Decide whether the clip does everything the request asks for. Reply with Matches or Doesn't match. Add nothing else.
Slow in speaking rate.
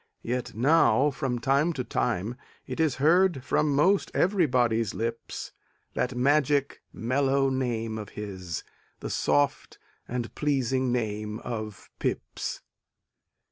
Matches